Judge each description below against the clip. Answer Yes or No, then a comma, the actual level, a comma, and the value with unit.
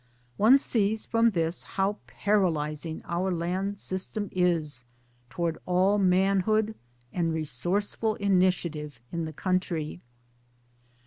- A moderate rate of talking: No, slow, 105 wpm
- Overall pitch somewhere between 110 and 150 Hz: No, medium, 185 Hz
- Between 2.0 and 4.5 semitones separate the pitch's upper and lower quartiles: Yes, average, 3.6 semitones